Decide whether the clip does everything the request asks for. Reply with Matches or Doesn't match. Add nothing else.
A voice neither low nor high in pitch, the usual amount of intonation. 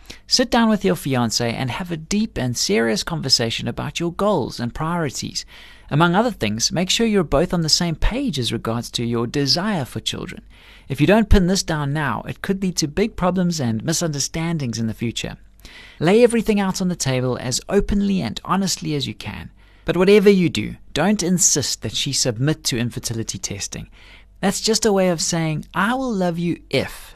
Doesn't match